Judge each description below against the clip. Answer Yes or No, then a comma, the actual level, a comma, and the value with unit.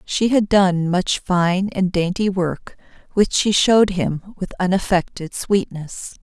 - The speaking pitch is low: No, medium, 185 Hz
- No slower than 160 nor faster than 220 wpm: No, average, 145 wpm